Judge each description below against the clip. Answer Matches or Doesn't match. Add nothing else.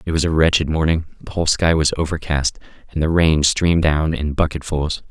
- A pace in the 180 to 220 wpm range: Matches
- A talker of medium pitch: Doesn't match